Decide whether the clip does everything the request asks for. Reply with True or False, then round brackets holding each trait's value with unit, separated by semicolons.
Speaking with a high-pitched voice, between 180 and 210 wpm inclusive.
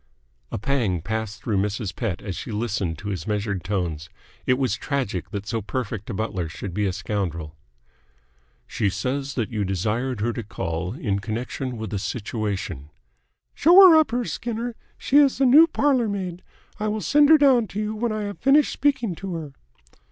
False (115 Hz; 190 wpm)